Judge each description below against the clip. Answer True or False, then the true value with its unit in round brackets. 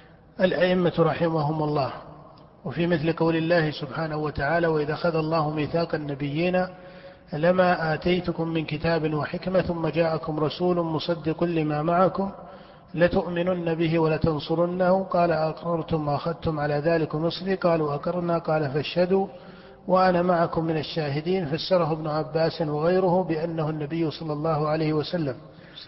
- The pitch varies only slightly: True (2.2 semitones)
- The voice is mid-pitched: True (165 Hz)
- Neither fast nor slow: True (120 wpm)